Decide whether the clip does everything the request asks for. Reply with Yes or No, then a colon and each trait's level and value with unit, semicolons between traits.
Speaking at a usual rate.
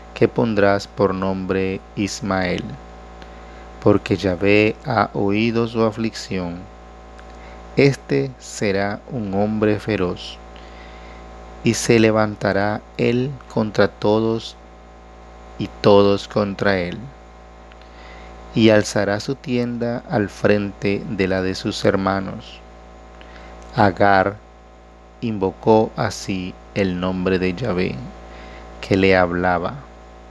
No: slow, 95 wpm